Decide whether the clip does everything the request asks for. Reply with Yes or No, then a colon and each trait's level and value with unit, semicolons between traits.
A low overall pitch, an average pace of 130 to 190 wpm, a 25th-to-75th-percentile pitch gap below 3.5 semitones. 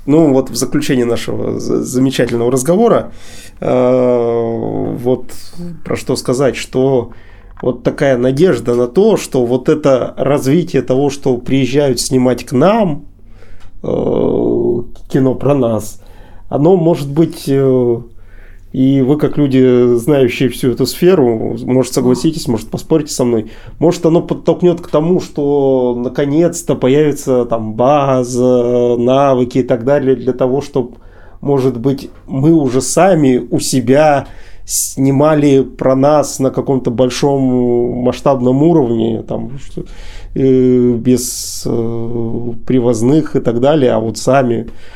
No: low, 130 Hz; average, 120 wpm; average, 3.1 semitones